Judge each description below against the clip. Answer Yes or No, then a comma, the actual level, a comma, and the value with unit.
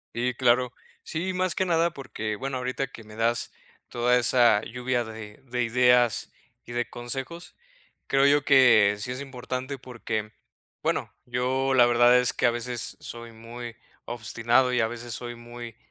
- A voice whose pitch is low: Yes, low, 120 Hz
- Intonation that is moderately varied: No, narrow, 1.6 semitones